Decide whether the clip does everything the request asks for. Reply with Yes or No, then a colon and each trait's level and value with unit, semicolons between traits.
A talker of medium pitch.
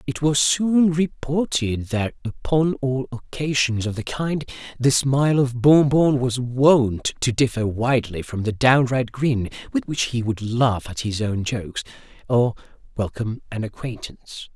No: low, 125 Hz